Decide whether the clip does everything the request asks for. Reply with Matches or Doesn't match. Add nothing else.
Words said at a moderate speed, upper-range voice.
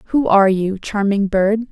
Matches